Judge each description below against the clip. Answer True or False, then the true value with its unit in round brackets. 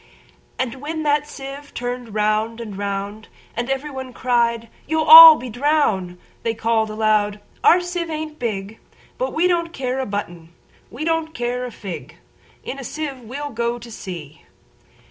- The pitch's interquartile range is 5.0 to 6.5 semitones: True (5.5 semitones)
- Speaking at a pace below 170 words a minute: True (150 wpm)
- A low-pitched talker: False (245 Hz)